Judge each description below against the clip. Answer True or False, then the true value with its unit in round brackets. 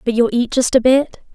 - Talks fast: True (265 wpm)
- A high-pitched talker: True (245 Hz)